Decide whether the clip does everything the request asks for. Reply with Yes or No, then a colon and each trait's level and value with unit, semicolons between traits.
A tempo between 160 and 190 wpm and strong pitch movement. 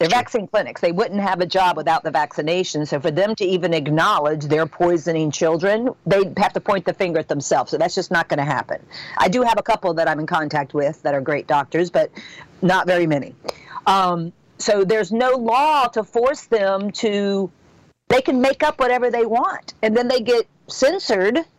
No: fast, 205 wpm; wide, 5.7 semitones